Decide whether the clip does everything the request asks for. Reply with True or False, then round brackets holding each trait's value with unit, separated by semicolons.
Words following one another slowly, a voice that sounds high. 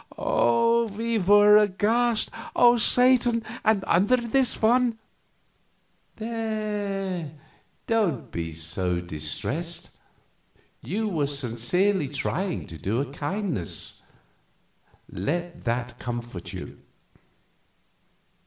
True (90 wpm; 195 Hz)